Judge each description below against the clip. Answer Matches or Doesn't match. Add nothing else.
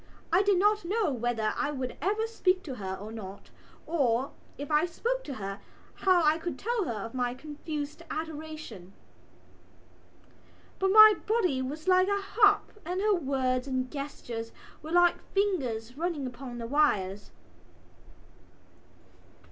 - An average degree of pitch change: Doesn't match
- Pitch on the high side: Matches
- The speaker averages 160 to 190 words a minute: Doesn't match